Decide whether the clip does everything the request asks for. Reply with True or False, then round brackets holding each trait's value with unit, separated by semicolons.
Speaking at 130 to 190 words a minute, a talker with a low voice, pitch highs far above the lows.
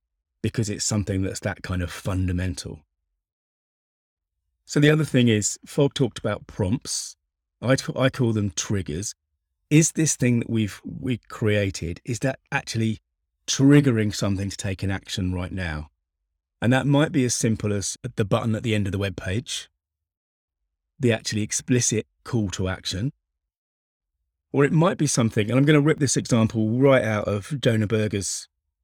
True (165 wpm; 105 Hz; 7.2 semitones)